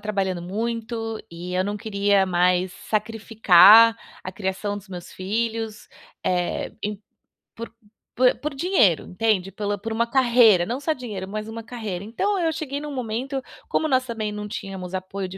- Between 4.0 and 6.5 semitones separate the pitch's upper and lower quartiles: No, average, 3.5 semitones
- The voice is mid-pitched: No, high, 215 Hz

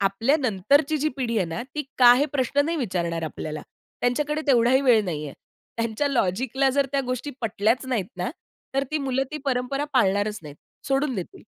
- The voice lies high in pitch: Yes, very high, 250 Hz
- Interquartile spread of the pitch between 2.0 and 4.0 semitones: No, average, 5.3 semitones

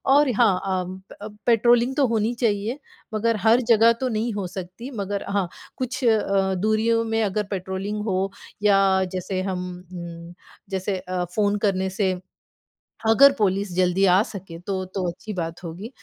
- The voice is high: Yes, high, 200 Hz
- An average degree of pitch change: Yes, average, 3.2 semitones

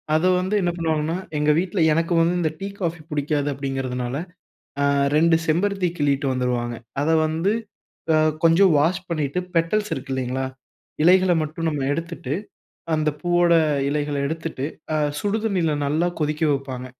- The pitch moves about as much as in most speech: Yes, average, 3.5 semitones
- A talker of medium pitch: Yes, medium, 160 Hz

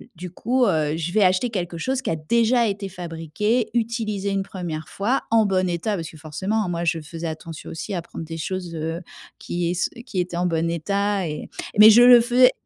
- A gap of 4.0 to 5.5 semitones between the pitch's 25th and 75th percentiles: Yes, average, 4.7 semitones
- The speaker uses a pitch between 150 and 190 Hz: Yes, medium, 185 Hz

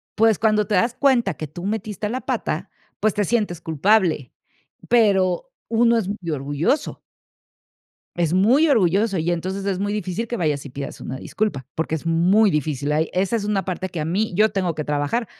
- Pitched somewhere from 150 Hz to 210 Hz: Yes, high, 190 Hz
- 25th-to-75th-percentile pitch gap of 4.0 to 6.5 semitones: Yes, average, 5.0 semitones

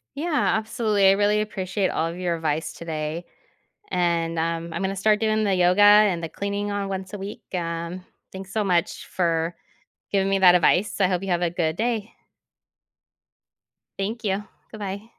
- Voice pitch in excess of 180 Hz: Yes, high, 190 Hz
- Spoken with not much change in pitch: No, average, 3.3 semitones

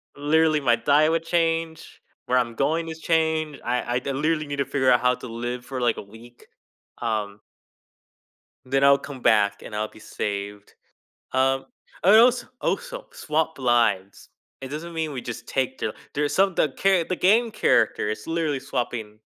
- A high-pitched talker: No, low, 135 Hz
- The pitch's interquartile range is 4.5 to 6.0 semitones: Yes, average, 5.1 semitones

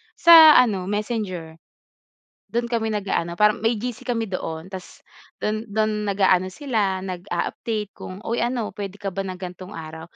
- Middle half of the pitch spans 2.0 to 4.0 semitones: Yes, average, 3.2 semitones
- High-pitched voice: Yes, high, 205 Hz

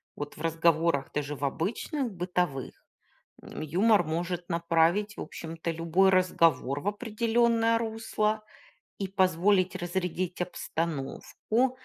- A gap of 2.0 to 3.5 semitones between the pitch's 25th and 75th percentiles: No, average, 4.3 semitones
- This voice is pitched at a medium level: Yes, medium, 180 Hz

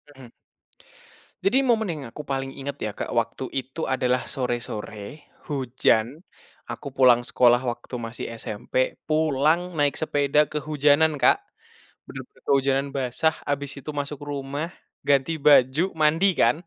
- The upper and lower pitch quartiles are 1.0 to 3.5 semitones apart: Yes, average, 2.9 semitones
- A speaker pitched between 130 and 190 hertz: Yes, medium, 140 Hz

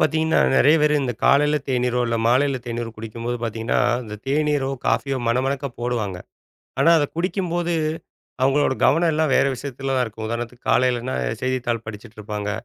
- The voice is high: No, low, 130 Hz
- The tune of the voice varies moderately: Yes, average, 3.7 semitones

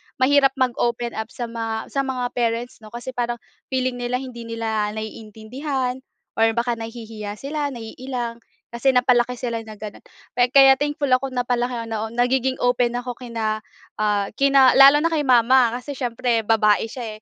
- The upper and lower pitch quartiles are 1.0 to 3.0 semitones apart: Yes, narrow, 2.4 semitones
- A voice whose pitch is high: Yes, high, 240 Hz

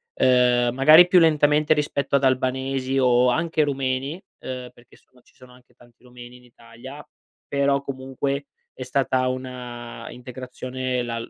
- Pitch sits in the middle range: No, low, 130 Hz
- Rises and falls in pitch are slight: Yes, narrow, 1.9 semitones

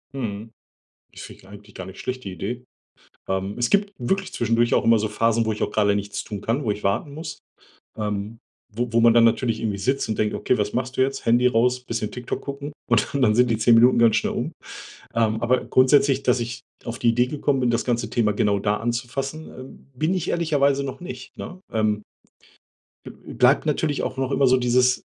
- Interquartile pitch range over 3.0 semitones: Yes, average, 3.5 semitones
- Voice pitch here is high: No, low, 120 Hz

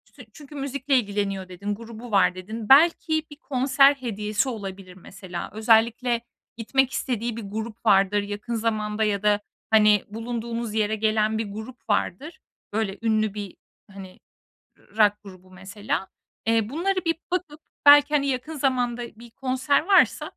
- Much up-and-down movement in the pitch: No, average, 4.0 semitones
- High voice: Yes, high, 225 Hz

